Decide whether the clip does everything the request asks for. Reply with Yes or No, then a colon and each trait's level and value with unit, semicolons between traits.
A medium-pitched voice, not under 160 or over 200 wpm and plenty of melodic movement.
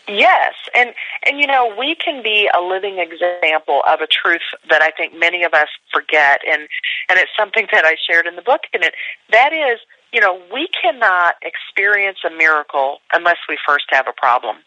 Yes: medium, 180 Hz; average, 195 wpm; wide, 7.5 semitones